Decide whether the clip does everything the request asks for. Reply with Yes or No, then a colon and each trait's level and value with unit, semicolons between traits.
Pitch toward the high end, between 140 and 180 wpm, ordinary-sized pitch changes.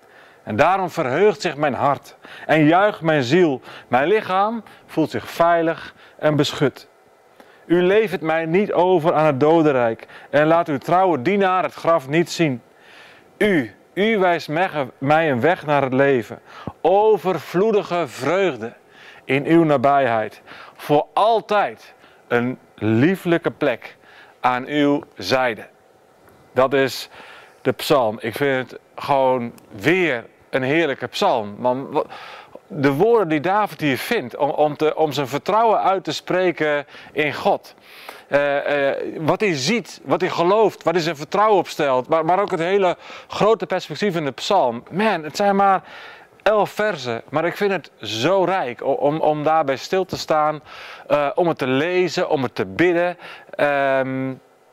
No: medium, 155 Hz; average, 150 wpm; average, 4.8 semitones